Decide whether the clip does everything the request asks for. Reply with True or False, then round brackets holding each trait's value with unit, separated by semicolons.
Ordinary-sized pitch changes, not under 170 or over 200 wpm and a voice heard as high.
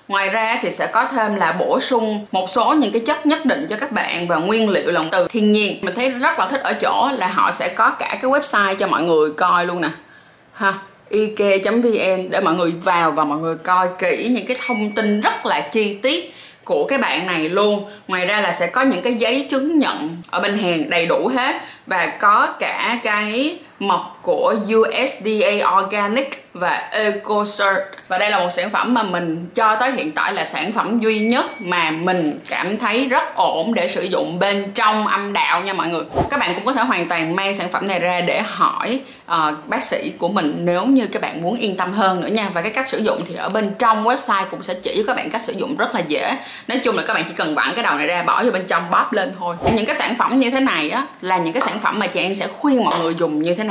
False (4.9 semitones; 250 wpm; 205 Hz)